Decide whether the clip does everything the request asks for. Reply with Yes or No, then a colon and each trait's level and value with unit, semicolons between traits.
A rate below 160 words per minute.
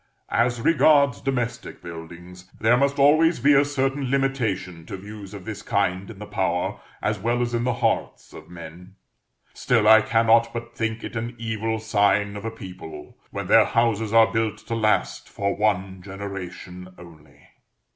No: average, 165 wpm